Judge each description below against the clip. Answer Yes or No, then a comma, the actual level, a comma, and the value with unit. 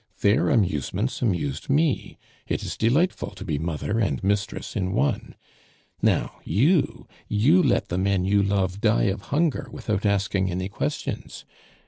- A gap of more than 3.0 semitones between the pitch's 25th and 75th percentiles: Yes, average, 4.2 semitones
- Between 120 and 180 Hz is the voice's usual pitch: No, low, 100 Hz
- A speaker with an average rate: Yes, average, 145 wpm